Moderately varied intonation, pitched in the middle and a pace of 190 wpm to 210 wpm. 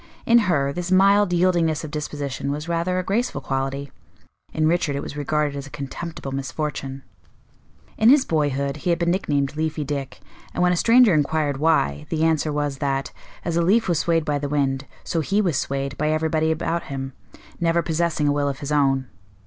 Yes: average, 3.4 semitones; medium, 150 Hz; average, 195 wpm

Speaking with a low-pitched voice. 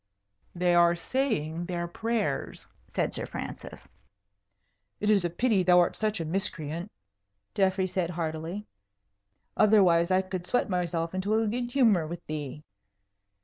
No: medium, 180 Hz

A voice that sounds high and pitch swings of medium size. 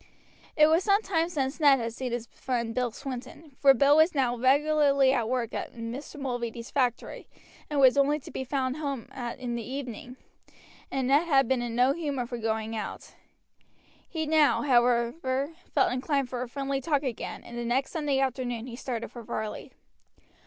Yes: very high, 260 Hz; average, 3.0 semitones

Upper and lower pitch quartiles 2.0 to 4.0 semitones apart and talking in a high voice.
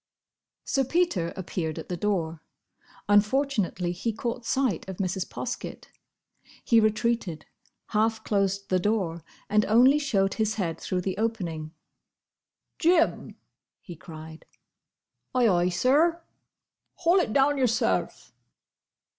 No: wide, 5.6 semitones; high, 210 Hz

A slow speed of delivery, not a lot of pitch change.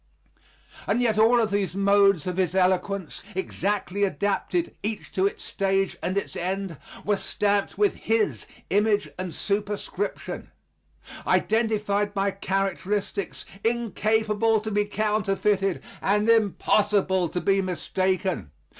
Yes: slow, 115 wpm; narrow, 1.7 semitones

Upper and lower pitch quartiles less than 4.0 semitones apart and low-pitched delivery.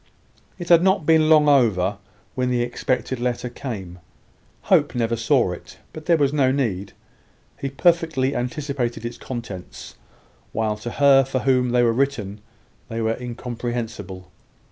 Yes: average, 3.6 semitones; low, 125 Hz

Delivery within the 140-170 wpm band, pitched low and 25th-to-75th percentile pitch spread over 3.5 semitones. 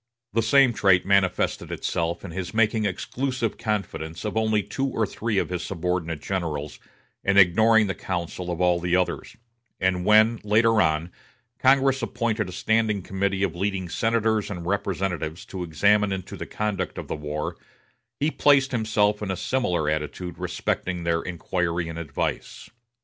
Yes: average, 160 wpm; very low, 95 Hz; average, 4.0 semitones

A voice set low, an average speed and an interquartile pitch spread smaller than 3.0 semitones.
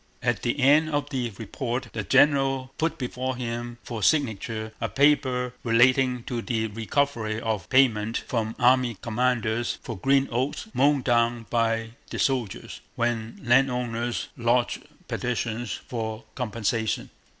No: low, 120 Hz; slow, 130 wpm; narrow, 2.4 semitones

